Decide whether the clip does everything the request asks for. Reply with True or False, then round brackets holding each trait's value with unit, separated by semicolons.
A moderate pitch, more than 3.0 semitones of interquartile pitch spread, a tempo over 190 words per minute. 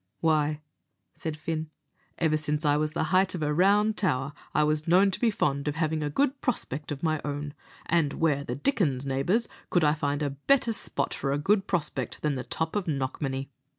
True (155 Hz; 3.6 semitones; 205 wpm)